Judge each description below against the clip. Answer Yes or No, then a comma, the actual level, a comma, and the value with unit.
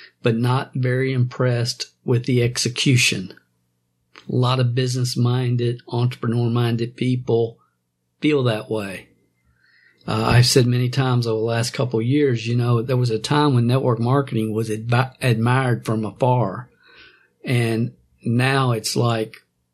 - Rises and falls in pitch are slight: Yes, narrow, 2.1 semitones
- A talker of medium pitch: No, low, 120 Hz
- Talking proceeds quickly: No, average, 140 wpm